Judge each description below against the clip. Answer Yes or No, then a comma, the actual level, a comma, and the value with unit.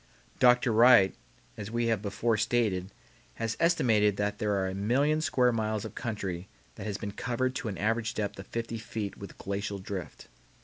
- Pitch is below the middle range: Yes, low, 110 Hz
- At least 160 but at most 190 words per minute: Yes, average, 180 wpm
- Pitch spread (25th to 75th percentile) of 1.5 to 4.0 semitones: Yes, average, 2.9 semitones